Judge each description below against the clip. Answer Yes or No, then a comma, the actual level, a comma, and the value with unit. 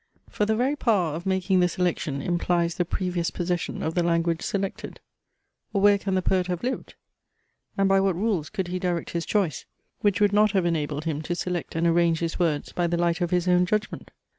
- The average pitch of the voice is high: No, medium, 180 Hz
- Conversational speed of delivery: No, fast, 215 wpm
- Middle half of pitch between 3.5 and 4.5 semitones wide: No, narrow, 2.4 semitones